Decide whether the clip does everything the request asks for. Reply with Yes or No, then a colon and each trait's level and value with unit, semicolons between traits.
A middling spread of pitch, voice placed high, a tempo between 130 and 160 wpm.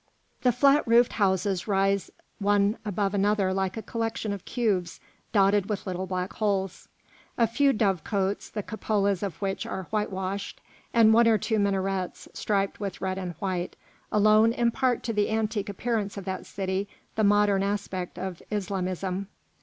No: narrow, 2.2 semitones; high, 200 Hz; average, 155 wpm